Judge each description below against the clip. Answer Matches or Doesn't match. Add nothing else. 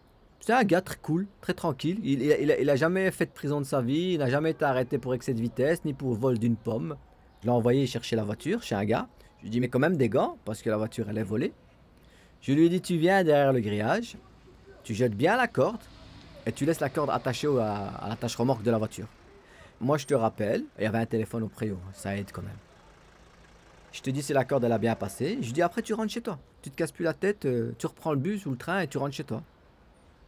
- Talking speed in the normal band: Doesn't match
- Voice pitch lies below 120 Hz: Doesn't match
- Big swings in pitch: Matches